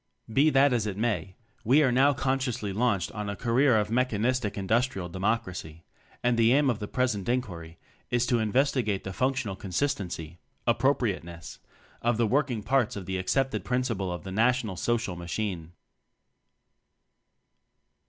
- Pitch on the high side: No, low, 115 Hz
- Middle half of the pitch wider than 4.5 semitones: Yes, average, 4.9 semitones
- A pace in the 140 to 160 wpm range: Yes, average, 155 wpm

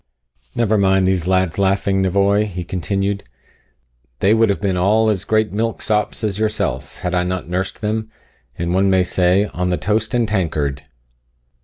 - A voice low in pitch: Yes, very low, 95 Hz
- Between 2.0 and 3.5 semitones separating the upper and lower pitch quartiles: Yes, average, 2.7 semitones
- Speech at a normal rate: Yes, average, 165 wpm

